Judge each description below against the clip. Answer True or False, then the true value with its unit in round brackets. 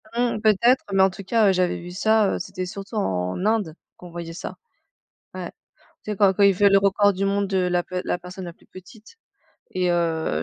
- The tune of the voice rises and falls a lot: False (2.4 semitones)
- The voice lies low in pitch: False (190 Hz)